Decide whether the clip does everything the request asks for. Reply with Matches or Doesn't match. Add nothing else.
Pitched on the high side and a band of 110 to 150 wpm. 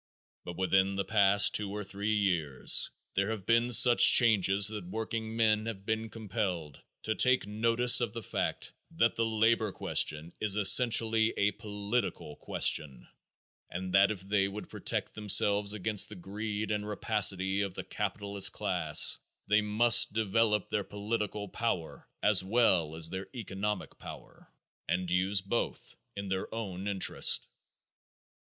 Doesn't match